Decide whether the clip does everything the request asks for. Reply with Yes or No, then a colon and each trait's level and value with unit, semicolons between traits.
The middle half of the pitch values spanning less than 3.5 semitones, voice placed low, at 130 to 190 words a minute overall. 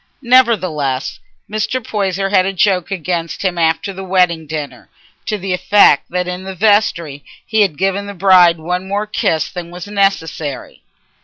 No: average, 3.0 semitones; medium, 185 Hz; average, 160 wpm